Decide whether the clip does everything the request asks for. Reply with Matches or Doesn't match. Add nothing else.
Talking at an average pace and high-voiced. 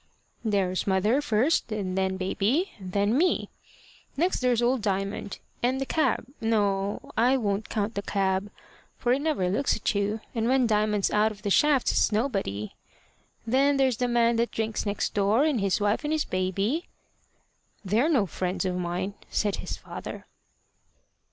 Matches